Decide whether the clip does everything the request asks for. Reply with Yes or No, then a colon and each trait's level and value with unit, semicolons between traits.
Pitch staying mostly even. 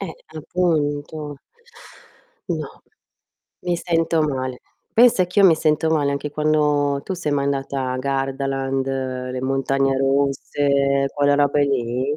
Yes: narrow, 2.2 semitones